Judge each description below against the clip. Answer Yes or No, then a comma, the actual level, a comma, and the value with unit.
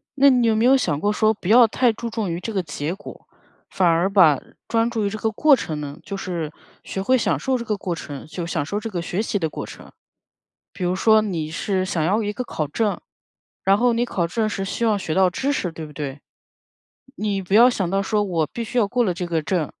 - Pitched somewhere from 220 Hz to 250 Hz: No, high, 195 Hz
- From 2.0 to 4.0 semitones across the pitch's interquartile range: No, average, 4.8 semitones